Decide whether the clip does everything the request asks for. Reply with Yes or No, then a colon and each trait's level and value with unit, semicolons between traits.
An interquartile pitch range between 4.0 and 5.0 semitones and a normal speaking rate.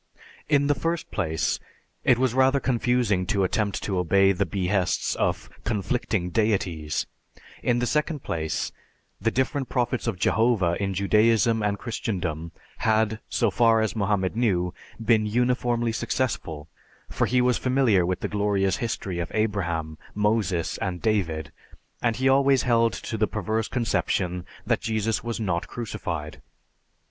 Yes: average, 4.4 semitones; average, 145 wpm